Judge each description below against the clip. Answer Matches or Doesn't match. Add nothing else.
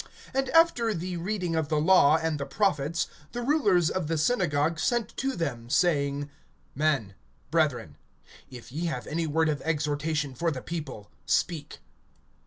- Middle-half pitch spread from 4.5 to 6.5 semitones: Doesn't match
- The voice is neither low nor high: Matches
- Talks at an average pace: Matches